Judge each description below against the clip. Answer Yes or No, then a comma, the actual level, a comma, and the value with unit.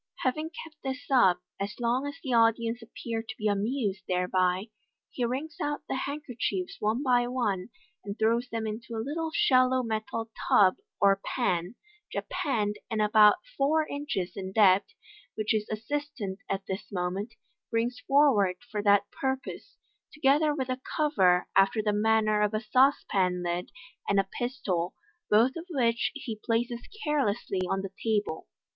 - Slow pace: No, average, 155 wpm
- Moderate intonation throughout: Yes, average, 4.4 semitones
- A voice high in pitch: Yes, high, 225 Hz